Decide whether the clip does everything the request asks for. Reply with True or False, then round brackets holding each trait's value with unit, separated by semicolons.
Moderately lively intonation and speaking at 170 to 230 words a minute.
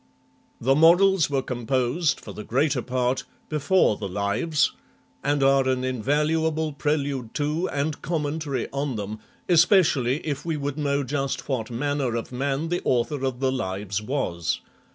False (3.3 semitones; 155 wpm)